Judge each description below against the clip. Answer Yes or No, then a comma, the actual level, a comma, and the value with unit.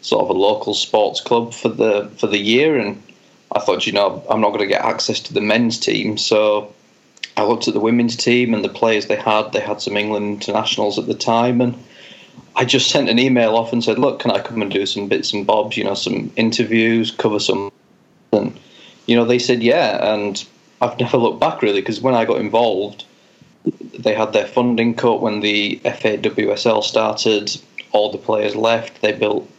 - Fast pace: Yes, fast, 210 wpm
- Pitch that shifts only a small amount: Yes, narrow, 2.2 semitones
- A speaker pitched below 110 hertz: No, low, 115 Hz